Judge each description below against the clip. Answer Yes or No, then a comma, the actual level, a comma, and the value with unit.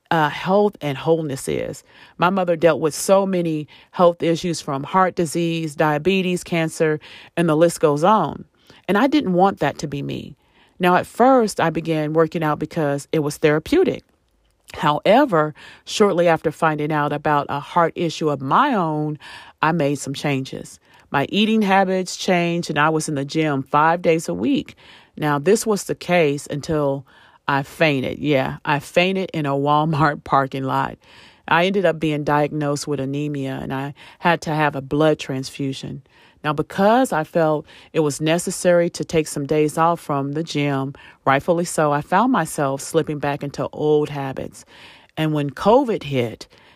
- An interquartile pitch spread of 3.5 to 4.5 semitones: No, average, 3.0 semitones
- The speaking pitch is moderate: Yes, medium, 155 Hz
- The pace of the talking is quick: No, average, 170 wpm